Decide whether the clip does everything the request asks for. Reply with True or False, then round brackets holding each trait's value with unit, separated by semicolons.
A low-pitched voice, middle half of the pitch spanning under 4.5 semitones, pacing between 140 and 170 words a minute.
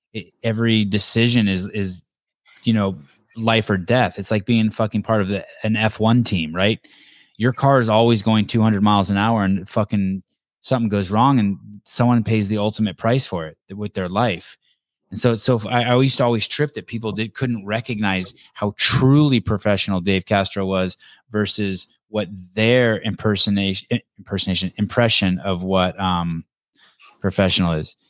True (105 Hz; 2.8 semitones; 165 wpm)